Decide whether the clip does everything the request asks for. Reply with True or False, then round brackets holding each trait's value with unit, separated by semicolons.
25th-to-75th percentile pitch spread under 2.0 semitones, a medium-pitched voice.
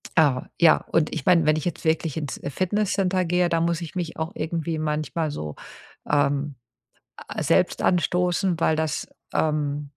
False (2.6 semitones; 160 Hz)